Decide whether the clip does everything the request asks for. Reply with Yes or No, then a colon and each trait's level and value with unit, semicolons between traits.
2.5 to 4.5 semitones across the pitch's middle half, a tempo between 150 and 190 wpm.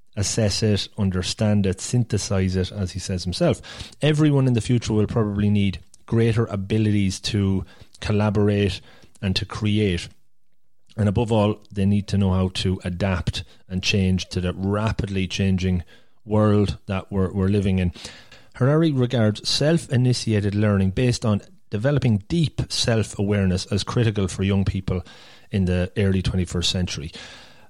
No: average, 2.8 semitones; average, 140 wpm